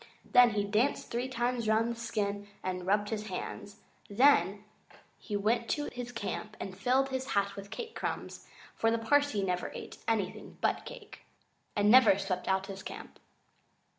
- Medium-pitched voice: No, high, 215 Hz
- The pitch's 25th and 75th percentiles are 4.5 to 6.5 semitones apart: No, average, 3.4 semitones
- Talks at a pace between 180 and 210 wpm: No, average, 165 wpm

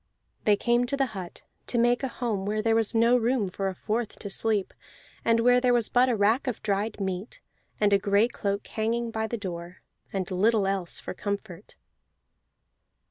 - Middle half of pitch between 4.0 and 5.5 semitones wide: No, average, 3.1 semitones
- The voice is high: Yes, high, 220 Hz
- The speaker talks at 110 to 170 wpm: No, average, 190 wpm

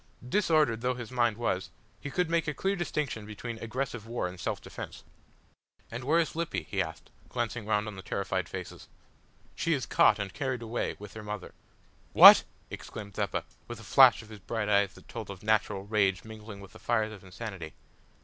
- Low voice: Yes, low, 110 Hz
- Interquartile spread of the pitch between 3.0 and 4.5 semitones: Yes, average, 3.6 semitones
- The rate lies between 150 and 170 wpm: No, average, 195 wpm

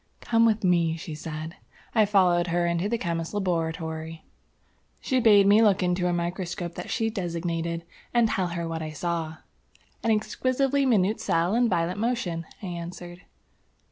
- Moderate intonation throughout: Yes, average, 4.0 semitones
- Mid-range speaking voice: Yes, medium, 175 Hz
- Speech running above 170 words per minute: No, average, 160 wpm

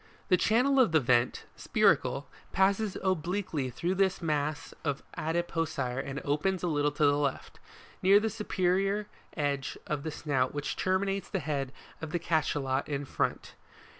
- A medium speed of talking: Yes, average, 160 wpm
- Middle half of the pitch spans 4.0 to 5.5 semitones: Yes, average, 4.9 semitones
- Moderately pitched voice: Yes, medium, 160 Hz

